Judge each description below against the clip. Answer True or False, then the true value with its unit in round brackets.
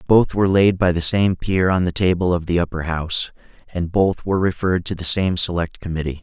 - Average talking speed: False (220 wpm)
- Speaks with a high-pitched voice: False (90 Hz)